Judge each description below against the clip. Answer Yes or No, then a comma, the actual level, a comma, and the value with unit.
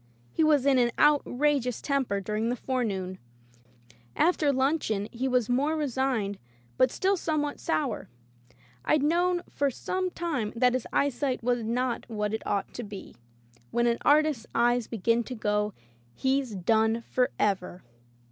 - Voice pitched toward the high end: Yes, very high, 250 Hz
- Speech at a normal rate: Yes, average, 145 wpm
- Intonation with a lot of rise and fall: No, average, 4.5 semitones